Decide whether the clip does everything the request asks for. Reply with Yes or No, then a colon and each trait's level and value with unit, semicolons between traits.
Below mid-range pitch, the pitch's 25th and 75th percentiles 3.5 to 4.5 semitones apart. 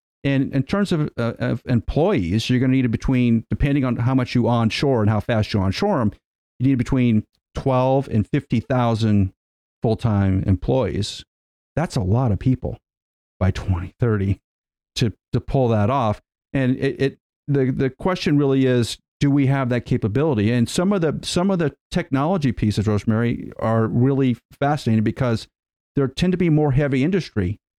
Yes: low, 125 Hz; average, 4.2 semitones